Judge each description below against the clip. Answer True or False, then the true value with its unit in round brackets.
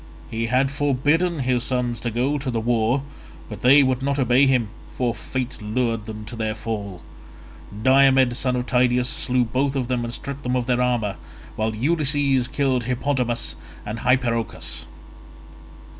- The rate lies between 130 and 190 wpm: True (160 wpm)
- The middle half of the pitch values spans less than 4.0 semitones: True (2.4 semitones)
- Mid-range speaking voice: False (125 Hz)